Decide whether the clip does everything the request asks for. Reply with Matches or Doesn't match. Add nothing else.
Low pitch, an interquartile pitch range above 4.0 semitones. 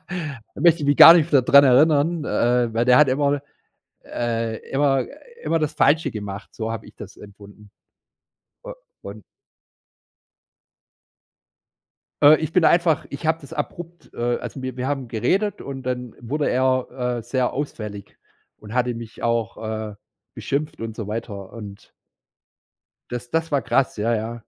Matches